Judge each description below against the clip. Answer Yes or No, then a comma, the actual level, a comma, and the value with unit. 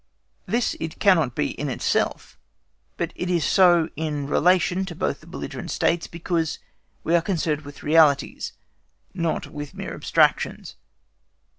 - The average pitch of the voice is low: No, medium, 165 Hz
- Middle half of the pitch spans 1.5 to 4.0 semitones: Yes, average, 3.1 semitones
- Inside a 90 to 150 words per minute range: Yes, average, 140 wpm